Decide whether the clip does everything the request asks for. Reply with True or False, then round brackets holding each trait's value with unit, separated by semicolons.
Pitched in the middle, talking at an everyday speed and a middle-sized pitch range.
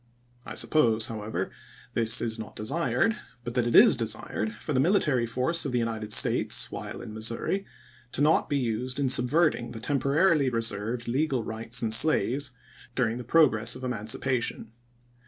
False (120 Hz; 160 wpm; 3.6 semitones)